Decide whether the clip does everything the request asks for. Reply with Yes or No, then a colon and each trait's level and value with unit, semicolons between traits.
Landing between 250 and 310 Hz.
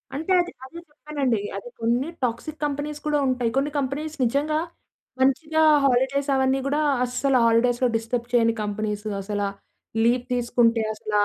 Yes: very high, 255 Hz